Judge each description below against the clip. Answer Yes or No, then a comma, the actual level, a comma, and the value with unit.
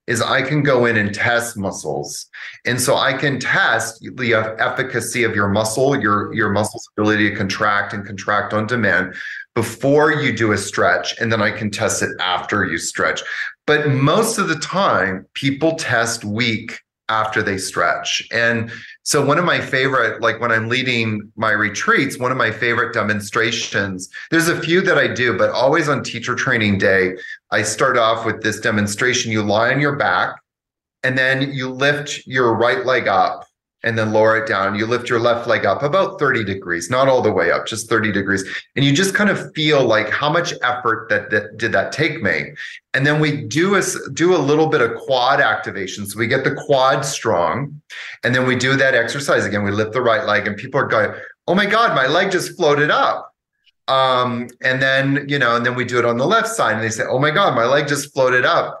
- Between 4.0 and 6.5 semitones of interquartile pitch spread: Yes, average, 4.7 semitones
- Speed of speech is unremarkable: No, fast, 210 wpm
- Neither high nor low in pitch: No, low, 120 Hz